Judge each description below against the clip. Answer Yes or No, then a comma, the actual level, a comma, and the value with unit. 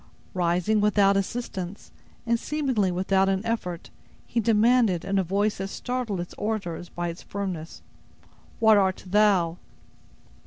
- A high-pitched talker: Yes, high, 195 Hz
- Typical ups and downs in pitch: Yes, average, 3.2 semitones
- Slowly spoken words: Yes, slow, 130 wpm